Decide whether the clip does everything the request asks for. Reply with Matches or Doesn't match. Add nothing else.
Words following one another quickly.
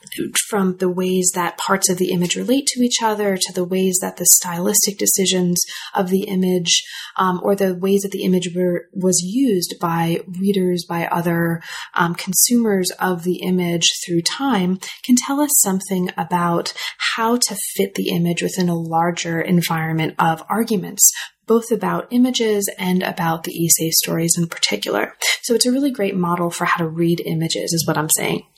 Doesn't match